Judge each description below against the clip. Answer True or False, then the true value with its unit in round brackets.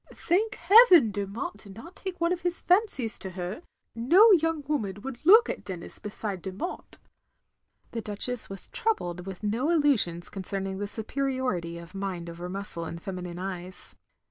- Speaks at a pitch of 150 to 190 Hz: False (210 Hz)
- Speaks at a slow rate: False (160 wpm)